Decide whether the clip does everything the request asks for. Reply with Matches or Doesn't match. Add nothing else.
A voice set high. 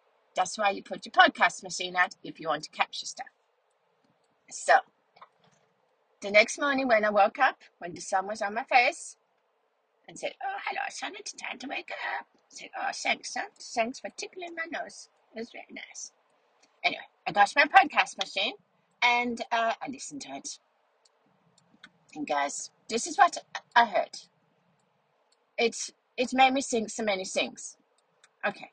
Matches